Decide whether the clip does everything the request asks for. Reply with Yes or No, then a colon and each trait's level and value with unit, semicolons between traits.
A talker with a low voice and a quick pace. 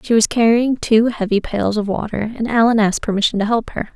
No: high, 220 Hz; fast, 230 wpm